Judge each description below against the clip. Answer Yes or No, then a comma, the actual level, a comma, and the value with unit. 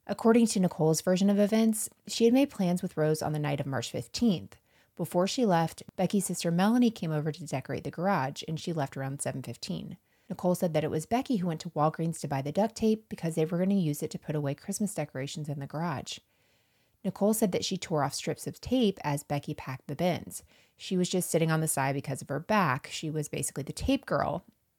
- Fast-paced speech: Yes, fast, 230 wpm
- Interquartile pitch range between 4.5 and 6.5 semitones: Yes, average, 5.2 semitones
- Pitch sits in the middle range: Yes, medium, 165 Hz